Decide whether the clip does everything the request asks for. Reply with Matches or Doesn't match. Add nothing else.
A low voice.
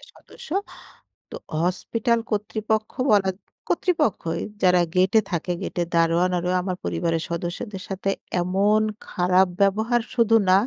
Doesn't match